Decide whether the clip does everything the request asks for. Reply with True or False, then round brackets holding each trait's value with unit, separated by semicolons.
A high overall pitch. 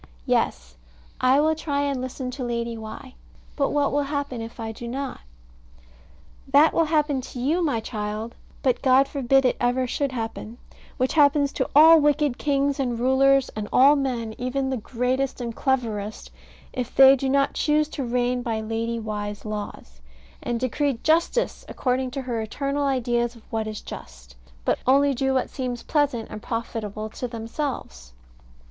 True (255 Hz)